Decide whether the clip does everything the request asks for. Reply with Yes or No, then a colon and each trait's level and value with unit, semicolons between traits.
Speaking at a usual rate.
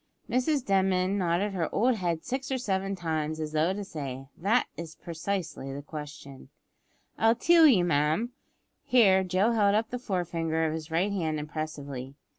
Yes: average, 170 wpm